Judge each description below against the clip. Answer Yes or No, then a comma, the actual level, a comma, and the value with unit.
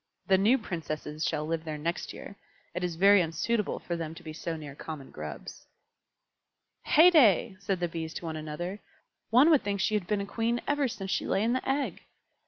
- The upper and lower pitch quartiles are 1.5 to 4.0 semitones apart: No, average, 5.2 semitones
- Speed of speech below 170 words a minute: No, average, 200 wpm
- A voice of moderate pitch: Yes, medium, 180 Hz